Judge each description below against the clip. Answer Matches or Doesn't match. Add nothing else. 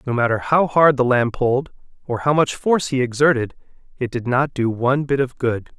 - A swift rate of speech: Matches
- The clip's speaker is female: Doesn't match